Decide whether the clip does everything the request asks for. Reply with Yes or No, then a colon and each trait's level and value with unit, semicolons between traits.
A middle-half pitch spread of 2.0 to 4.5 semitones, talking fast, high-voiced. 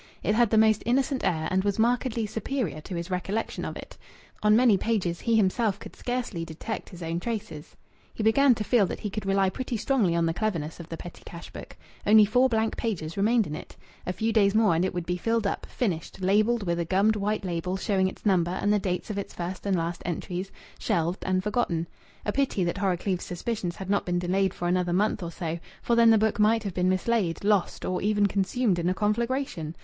Yes: average, 3.8 semitones; fast, 225 wpm; high, 200 Hz